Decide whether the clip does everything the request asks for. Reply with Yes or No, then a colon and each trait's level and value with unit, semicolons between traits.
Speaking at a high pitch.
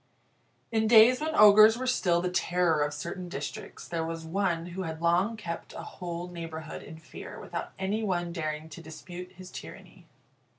No: medium, 175 Hz